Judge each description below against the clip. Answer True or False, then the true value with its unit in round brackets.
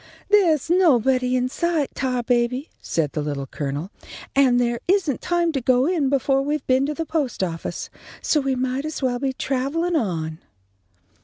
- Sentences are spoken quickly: False (165 wpm)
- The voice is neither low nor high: False (265 Hz)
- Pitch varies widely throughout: False (4.0 semitones)